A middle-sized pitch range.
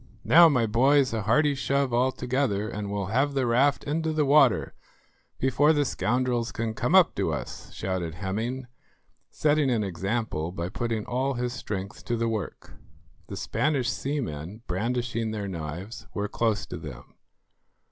Yes: average, 4.6 semitones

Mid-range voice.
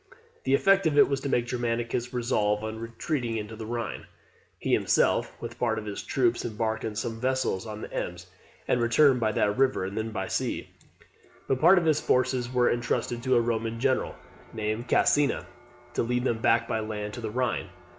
No: low, 120 Hz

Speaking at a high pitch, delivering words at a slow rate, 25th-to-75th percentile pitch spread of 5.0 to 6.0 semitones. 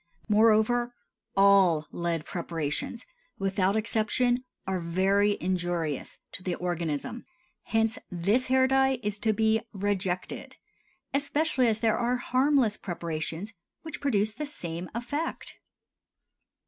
Yes: high, 210 Hz; slow, 110 wpm; wide, 5.4 semitones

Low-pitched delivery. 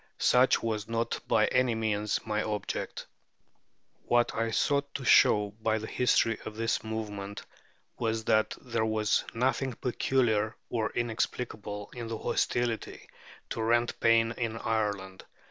Yes: low, 115 Hz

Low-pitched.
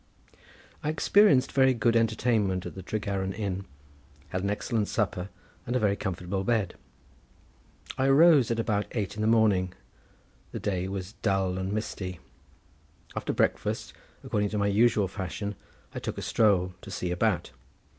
Yes: low, 100 Hz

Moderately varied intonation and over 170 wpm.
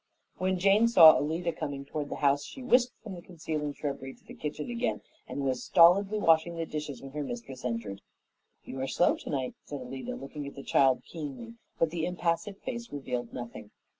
Yes: average, 4.9 semitones; average, 195 wpm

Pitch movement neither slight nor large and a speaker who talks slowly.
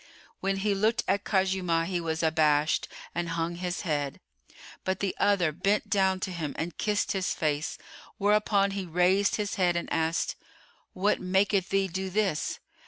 No: average, 3.0 semitones; average, 165 wpm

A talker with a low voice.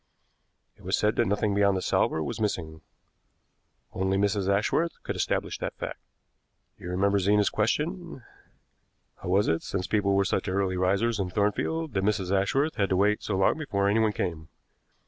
Yes: low, 100 Hz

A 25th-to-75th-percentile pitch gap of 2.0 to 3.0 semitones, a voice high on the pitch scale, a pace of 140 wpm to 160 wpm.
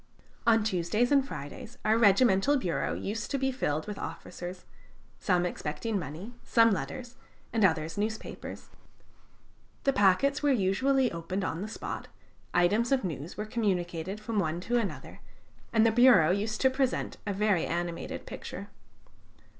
No: average, 5.2 semitones; high, 210 Hz; average, 145 wpm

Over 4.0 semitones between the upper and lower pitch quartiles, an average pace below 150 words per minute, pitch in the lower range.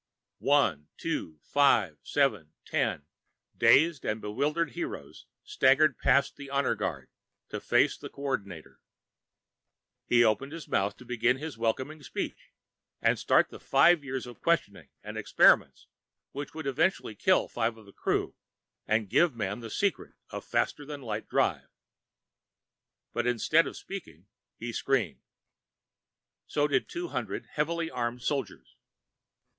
Yes: wide, 5.4 semitones; average, 140 wpm; low, 130 Hz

